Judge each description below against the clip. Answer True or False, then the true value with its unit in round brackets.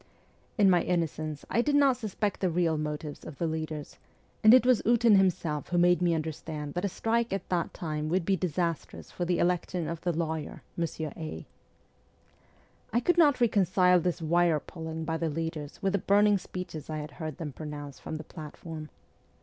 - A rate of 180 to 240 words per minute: True (190 wpm)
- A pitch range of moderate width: True (3.4 semitones)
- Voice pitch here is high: False (170 Hz)